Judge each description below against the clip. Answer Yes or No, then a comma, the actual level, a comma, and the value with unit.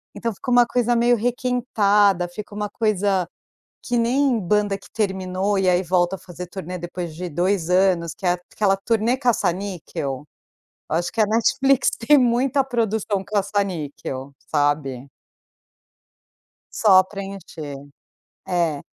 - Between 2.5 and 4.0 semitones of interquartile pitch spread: No, average, 4.4 semitones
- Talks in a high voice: Yes, high, 195 Hz